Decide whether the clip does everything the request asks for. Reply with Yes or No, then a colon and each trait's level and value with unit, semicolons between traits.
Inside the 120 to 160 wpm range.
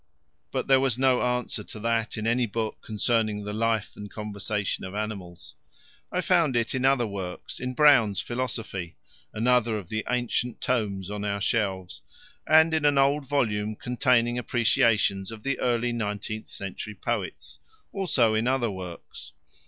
Yes: average, 155 wpm